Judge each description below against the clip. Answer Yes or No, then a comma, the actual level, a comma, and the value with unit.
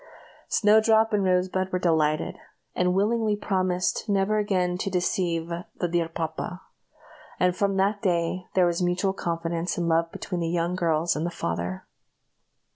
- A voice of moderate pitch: Yes, medium, 180 Hz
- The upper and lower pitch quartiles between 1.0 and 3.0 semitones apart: Yes, narrow, 2.5 semitones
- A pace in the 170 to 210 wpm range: No, average, 150 wpm